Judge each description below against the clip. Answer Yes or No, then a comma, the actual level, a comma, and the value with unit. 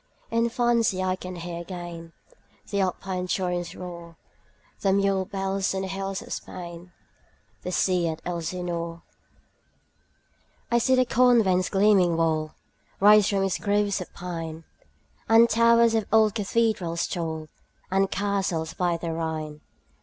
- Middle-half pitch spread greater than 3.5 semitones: No, average, 3.1 semitones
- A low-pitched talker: No, medium, 185 Hz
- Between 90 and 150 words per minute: Yes, average, 140 wpm